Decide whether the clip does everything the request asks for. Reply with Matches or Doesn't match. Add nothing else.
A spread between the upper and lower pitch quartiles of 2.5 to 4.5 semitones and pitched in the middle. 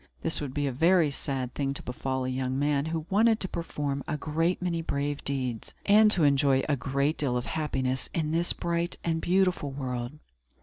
Matches